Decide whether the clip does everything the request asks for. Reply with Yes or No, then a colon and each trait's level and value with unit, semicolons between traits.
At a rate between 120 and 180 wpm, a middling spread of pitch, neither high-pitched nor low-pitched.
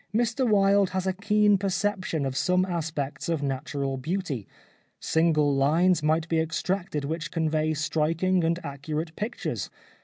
Yes: average, 140 wpm; average, 3.8 semitones; medium, 165 Hz